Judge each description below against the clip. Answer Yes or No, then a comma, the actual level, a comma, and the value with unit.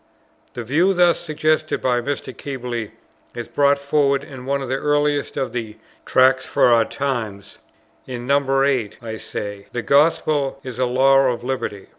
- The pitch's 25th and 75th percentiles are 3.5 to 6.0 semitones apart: No, average, 2.8 semitones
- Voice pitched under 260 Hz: Yes, low, 135 Hz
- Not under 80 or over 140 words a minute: No, average, 165 wpm